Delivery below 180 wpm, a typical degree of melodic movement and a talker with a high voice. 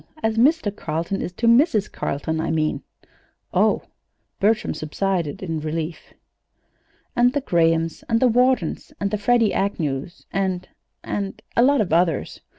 No: average, 140 wpm; wide, 5.8 semitones; high, 195 Hz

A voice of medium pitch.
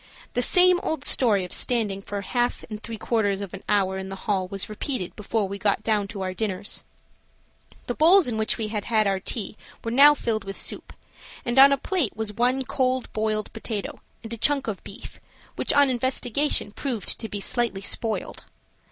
No: high, 220 Hz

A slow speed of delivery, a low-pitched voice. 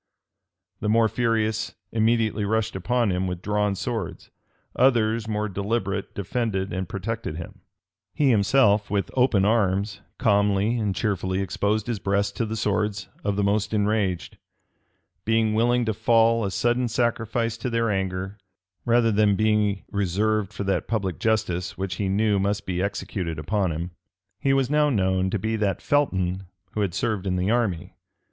No: average, 160 wpm; low, 105 Hz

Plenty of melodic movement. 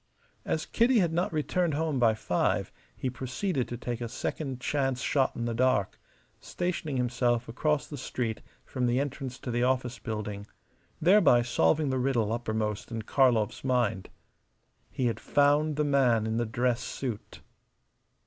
No: average, 3.5 semitones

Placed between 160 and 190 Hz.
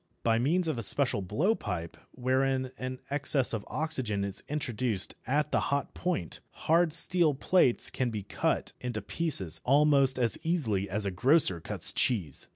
No: low, 130 Hz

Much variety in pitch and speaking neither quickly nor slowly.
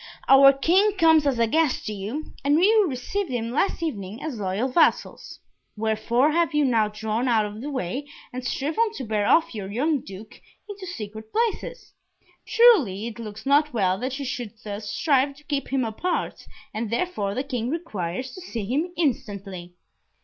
Yes: wide, 6.4 semitones; average, 180 wpm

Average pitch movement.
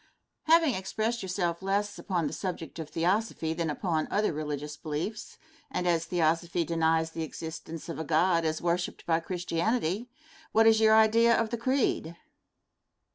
Yes: average, 4.9 semitones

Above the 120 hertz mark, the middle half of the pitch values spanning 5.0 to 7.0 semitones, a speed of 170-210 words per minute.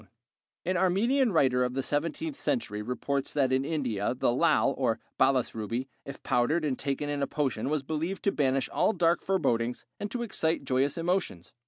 Yes: medium, 140 Hz; wide, 5.4 semitones; average, 185 wpm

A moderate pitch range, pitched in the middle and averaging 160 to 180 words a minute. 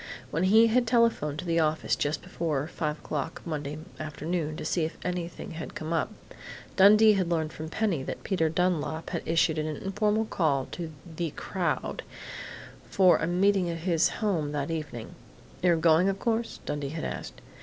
Yes: average, 3.4 semitones; medium, 165 Hz; average, 175 wpm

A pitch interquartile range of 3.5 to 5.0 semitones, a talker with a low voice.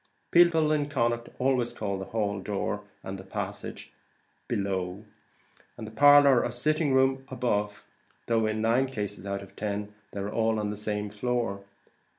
Yes: average, 4.1 semitones; low, 110 Hz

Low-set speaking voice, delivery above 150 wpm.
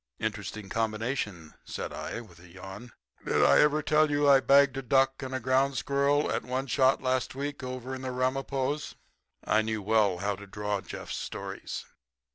Yes: low, 130 Hz; average, 175 wpm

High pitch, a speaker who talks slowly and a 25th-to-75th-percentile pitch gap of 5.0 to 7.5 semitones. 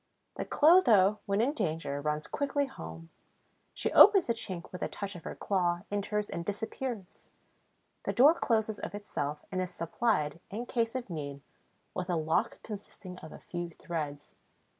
No: high, 195 Hz; average, 165 wpm; wide, 5.4 semitones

